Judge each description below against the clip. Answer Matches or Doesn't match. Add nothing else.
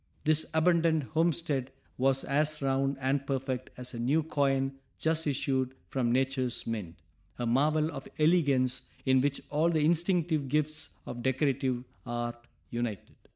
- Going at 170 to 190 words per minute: Doesn't match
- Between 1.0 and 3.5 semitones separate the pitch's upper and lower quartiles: Matches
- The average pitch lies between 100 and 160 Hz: Matches